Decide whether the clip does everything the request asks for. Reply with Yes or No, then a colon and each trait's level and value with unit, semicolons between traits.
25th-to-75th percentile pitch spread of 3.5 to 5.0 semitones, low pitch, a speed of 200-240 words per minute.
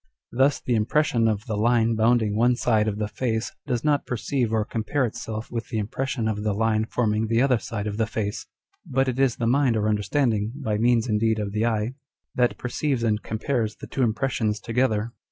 No: narrow, 2.5 semitones; low, 115 Hz; fast, 205 wpm